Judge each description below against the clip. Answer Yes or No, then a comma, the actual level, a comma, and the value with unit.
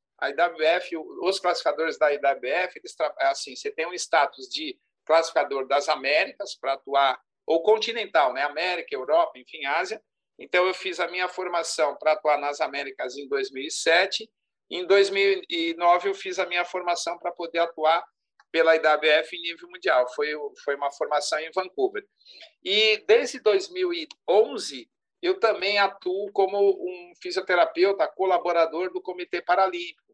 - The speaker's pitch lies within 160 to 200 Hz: Yes, medium, 185 Hz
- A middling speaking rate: Yes, average, 140 wpm